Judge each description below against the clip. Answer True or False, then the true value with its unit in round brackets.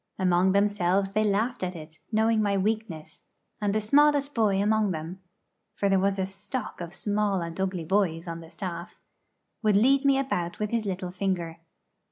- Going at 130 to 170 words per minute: False (180 wpm)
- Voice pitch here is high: True (195 Hz)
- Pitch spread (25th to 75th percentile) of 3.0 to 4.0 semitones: True (3.3 semitones)